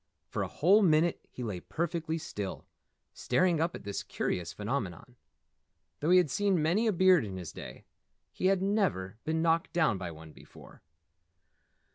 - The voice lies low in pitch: No, medium, 160 Hz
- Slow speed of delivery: No, average, 165 wpm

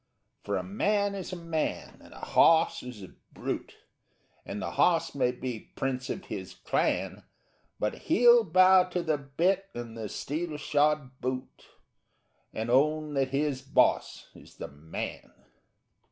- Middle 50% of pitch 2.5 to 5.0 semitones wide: No, wide, 5.6 semitones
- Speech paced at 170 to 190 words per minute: No, average, 150 wpm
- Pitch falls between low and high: Yes, medium, 145 Hz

